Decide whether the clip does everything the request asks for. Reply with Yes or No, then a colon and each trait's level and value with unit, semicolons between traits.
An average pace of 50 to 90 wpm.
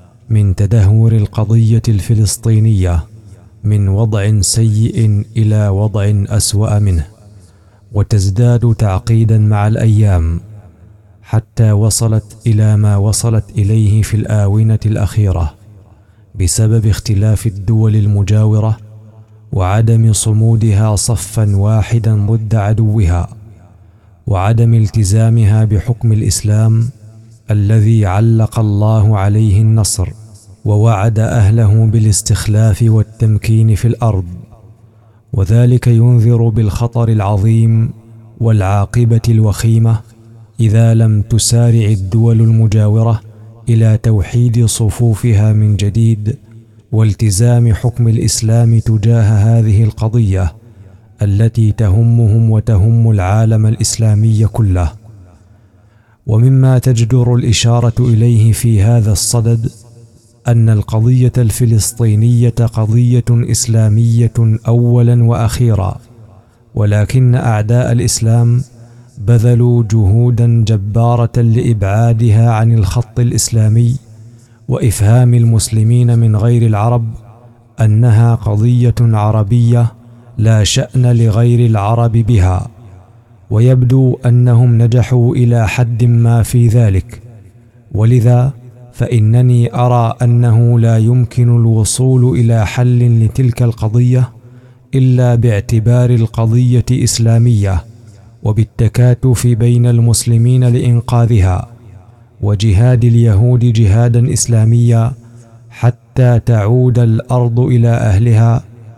Yes: average, 85 wpm